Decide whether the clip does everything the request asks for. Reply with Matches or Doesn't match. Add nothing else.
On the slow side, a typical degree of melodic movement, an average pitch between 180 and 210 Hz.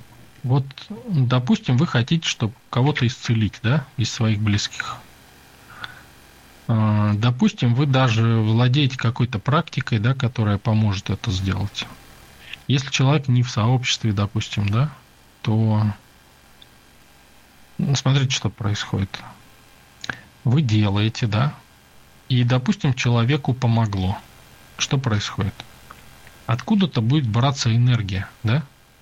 Doesn't match